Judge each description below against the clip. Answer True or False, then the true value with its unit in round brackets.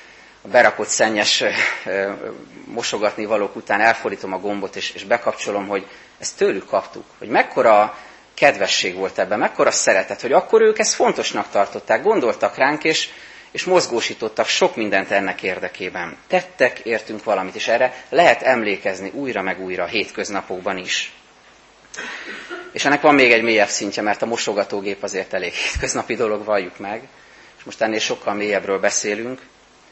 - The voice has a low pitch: True (105 Hz)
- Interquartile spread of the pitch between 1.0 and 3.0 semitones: False (5.1 semitones)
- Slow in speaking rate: False (150 wpm)